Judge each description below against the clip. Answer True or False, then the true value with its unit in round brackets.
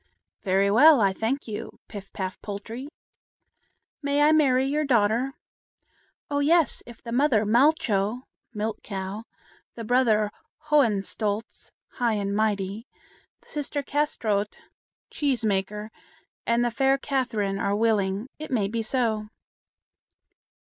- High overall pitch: True (225 Hz)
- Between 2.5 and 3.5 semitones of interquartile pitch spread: False (4.6 semitones)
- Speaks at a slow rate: True (120 wpm)